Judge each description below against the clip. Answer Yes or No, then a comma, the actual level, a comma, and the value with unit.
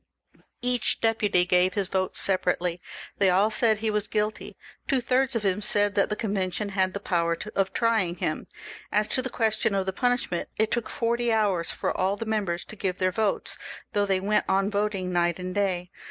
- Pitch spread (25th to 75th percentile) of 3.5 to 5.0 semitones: No, average, 2.8 semitones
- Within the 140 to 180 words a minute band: No, average, 200 wpm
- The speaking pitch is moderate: No, high, 200 Hz